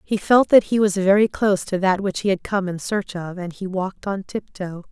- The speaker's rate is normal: No, fast, 255 wpm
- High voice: Yes, high, 195 Hz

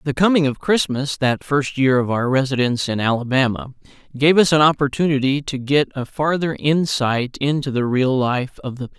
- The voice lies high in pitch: No, medium, 140 Hz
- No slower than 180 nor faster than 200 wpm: Yes, average, 185 wpm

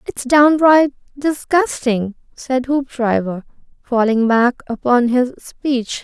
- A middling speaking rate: No, slow, 100 wpm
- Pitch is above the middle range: Yes, very high, 255 Hz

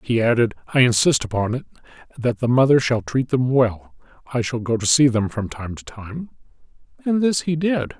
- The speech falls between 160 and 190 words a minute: No, fast, 205 wpm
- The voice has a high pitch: No, low, 125 Hz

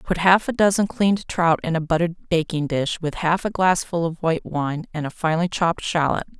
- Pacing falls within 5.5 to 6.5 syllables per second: Yes, 5.6 syllables/s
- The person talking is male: No, female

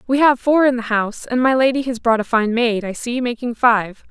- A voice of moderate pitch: No, high, 240 Hz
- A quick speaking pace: Yes, fast, 265 wpm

